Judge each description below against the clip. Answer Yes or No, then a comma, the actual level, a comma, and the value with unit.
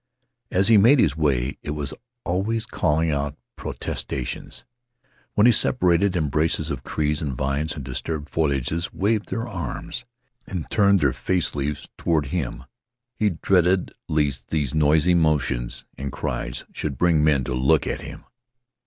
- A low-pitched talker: Yes, very low, 75 Hz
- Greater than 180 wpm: No, average, 150 wpm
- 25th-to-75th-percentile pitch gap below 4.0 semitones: No, average, 4.5 semitones